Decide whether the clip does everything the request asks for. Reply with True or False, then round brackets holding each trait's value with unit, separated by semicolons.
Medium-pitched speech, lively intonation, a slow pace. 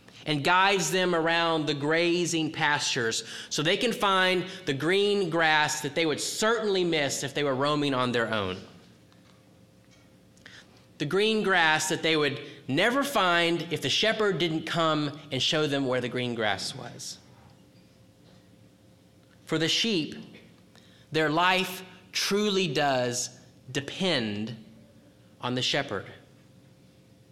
True (155 Hz; 6.1 semitones; 125 wpm)